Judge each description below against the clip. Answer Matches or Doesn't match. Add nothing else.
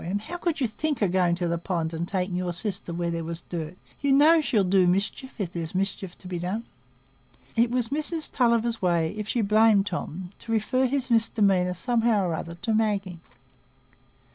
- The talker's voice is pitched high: Matches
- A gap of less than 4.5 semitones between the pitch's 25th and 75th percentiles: Doesn't match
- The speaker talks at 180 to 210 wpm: Matches